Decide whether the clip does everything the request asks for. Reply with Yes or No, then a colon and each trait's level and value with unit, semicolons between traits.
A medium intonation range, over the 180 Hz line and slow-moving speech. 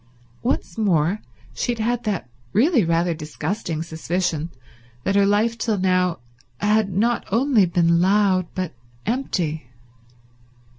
Yes: average, 4.4 semitones; high, 190 Hz; slow, 115 wpm